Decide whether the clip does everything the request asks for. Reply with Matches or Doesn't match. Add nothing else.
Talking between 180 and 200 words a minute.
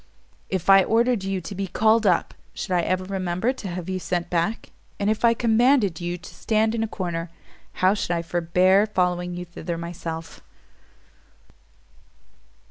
Doesn't match